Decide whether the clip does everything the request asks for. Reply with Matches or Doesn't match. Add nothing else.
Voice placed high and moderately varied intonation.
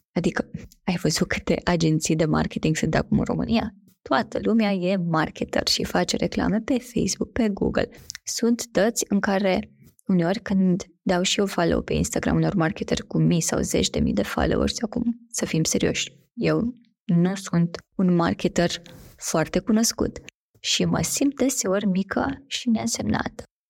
Matches